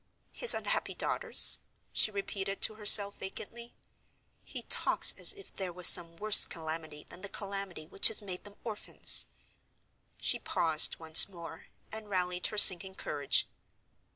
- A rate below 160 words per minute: Yes, average, 145 wpm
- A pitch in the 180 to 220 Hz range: Yes, high, 190 Hz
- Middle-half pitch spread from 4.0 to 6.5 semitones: No, average, 3.6 semitones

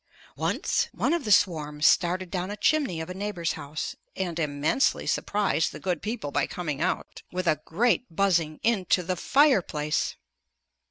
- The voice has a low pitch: No, medium, 180 Hz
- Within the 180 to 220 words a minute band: No, average, 160 wpm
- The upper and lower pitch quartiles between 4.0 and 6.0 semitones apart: Yes, average, 4.5 semitones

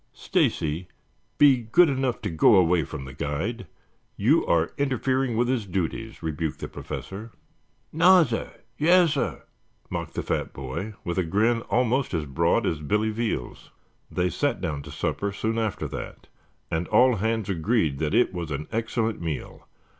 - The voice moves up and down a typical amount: No, wide, 6.8 semitones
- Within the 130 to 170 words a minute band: Yes, average, 155 wpm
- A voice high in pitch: No, low, 105 Hz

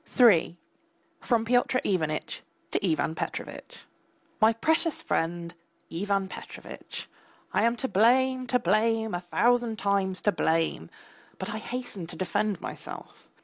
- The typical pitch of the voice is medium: No, high, 210 Hz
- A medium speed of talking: No, slow, 130 wpm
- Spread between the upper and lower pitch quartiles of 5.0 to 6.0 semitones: Yes, average, 5.3 semitones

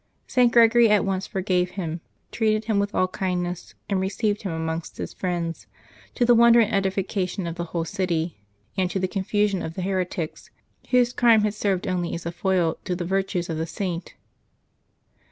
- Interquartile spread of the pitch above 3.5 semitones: No, average, 3.2 semitones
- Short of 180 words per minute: No, average, 185 wpm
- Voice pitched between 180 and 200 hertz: Yes, high, 190 Hz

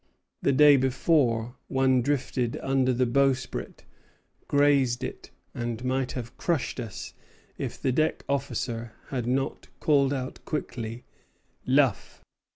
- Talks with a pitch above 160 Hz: No, low, 130 Hz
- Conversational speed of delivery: No, slow, 120 wpm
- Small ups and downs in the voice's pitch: Yes, narrow, 2.3 semitones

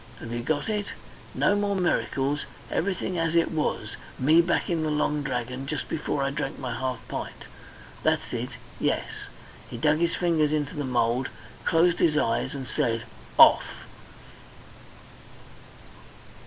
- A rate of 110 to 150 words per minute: Yes, average, 145 wpm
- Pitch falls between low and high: Yes, medium, 150 Hz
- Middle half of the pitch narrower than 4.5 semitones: Yes, average, 4.1 semitones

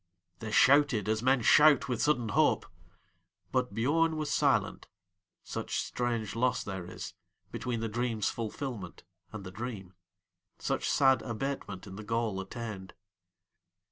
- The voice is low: Yes, low, 115 Hz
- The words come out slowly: Yes, slow, 120 wpm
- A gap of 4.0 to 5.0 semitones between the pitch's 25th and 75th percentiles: Yes, average, 4.5 semitones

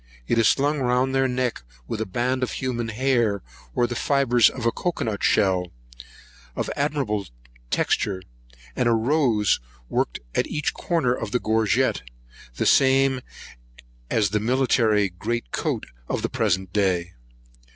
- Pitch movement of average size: Yes, average, 4.1 semitones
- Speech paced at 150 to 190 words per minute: No, average, 140 wpm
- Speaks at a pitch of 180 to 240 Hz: No, low, 120 Hz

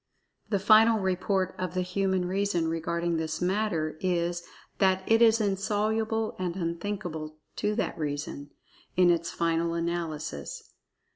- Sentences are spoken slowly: Yes, slow, 130 wpm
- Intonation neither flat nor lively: Yes, average, 3.3 semitones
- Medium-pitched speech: Yes, medium, 180 Hz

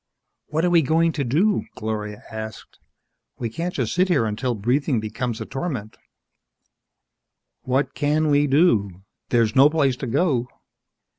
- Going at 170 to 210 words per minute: No, average, 150 wpm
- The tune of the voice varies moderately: No, wide, 5.8 semitones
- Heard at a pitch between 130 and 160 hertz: Yes, low, 135 Hz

